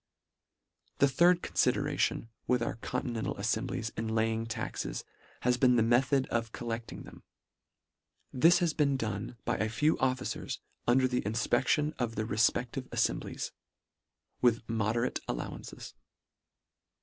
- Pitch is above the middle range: No, low, 120 Hz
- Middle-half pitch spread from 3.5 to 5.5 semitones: No, average, 2.7 semitones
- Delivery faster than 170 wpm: No, slow, 135 wpm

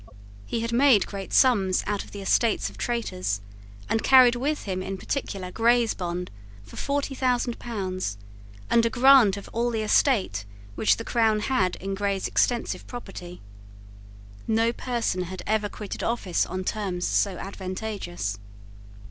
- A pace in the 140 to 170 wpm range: Yes, average, 150 wpm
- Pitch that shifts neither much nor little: Yes, average, 4.3 semitones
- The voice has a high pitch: Yes, high, 210 Hz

